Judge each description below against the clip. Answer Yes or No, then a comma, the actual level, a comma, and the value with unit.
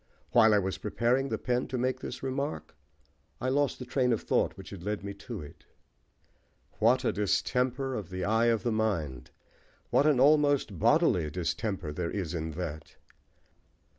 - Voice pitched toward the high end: No, low, 110 Hz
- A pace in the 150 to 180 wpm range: Yes, average, 170 wpm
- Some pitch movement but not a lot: No, wide, 5.7 semitones